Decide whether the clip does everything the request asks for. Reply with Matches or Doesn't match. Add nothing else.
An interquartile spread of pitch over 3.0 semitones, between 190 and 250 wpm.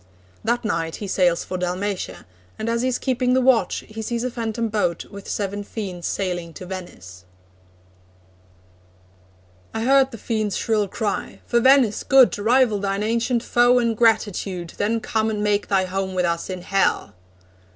Doesn't match